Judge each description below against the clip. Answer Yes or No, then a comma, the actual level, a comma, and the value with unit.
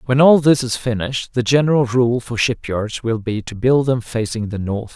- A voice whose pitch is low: Yes, low, 120 Hz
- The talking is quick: Yes, fast, 220 wpm